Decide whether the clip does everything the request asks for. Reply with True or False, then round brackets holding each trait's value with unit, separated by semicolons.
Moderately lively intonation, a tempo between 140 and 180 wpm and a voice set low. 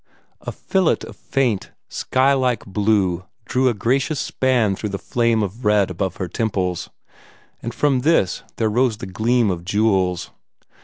True (4.7 semitones; 155 wpm; 110 Hz)